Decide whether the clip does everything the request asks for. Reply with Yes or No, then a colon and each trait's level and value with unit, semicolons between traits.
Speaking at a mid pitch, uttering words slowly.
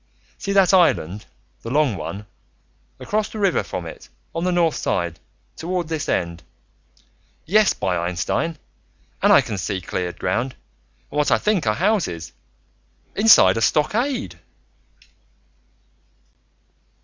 Yes: medium, 145 Hz; slow, 125 wpm